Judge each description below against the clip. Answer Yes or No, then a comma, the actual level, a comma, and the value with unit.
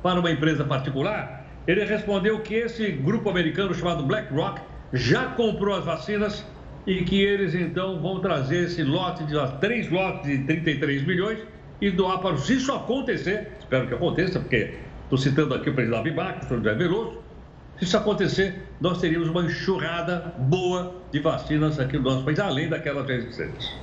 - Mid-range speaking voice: Yes, medium, 170 Hz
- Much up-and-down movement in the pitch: No, average, 4.8 semitones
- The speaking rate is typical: Yes, average, 170 wpm